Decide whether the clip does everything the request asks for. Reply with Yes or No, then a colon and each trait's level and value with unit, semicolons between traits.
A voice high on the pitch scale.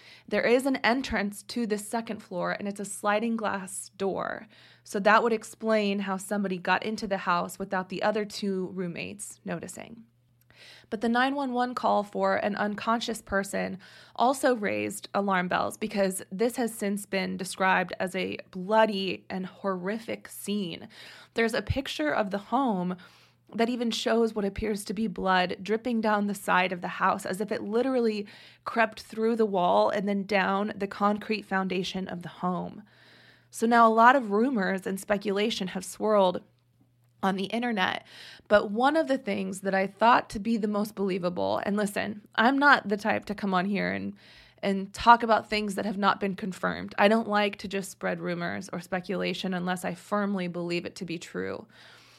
Yes: high, 205 Hz